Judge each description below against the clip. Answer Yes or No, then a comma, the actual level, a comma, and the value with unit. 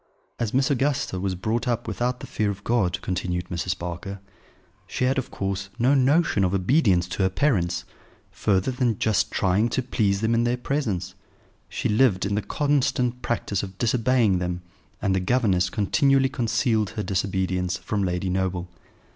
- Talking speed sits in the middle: Yes, average, 170 wpm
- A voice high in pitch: No, low, 105 Hz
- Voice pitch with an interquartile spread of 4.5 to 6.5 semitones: Yes, average, 5.0 semitones